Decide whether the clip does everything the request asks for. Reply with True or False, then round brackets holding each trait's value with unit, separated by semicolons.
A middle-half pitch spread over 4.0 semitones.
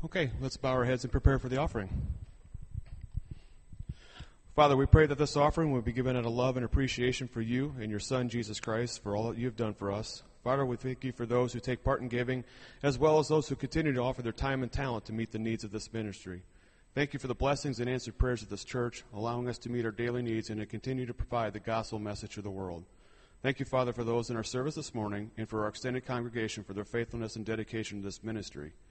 False (2.9 semitones)